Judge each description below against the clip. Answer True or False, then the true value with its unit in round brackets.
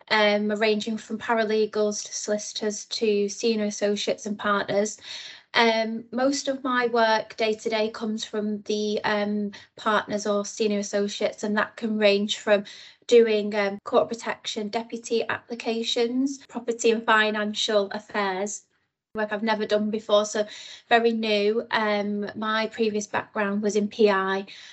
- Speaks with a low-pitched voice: False (215 Hz)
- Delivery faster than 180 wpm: False (140 wpm)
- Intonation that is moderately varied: False (1.5 semitones)